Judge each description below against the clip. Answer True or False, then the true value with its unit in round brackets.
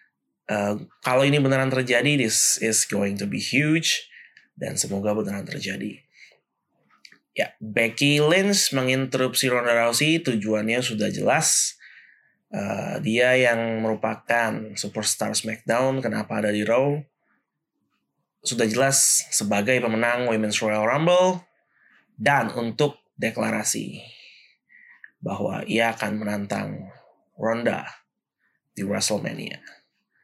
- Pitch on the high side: False (115 Hz)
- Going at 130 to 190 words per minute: False (100 wpm)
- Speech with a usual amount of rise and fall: True (4.0 semitones)